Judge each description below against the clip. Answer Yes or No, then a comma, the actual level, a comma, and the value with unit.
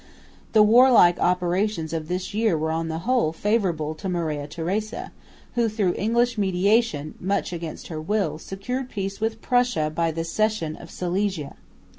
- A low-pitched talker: No, medium, 185 Hz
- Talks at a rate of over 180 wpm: No, average, 155 wpm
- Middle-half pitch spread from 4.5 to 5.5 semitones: Yes, average, 4.9 semitones